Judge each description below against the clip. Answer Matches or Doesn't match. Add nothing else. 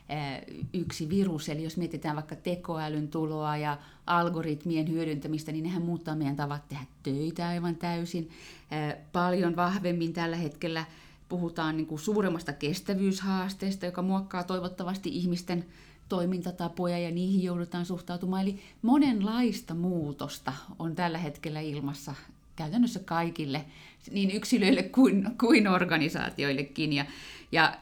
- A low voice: Doesn't match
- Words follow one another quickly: Doesn't match